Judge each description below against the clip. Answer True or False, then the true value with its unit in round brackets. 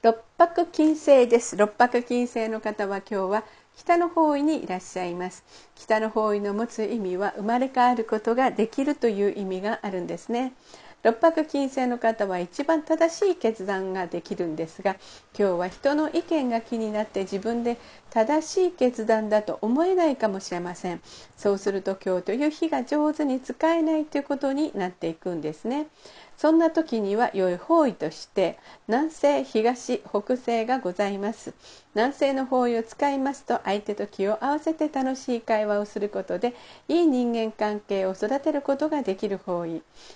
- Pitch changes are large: True (5.8 semitones)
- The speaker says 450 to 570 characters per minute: False (340 characters per minute)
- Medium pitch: False (230 Hz)